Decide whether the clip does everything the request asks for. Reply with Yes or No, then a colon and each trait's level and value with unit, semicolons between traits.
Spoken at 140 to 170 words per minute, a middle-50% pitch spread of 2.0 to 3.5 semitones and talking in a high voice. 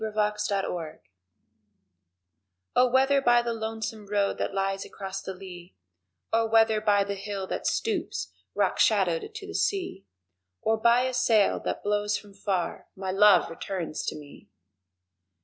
Yes: average, 155 wpm; average, 3.0 semitones; high, 210 Hz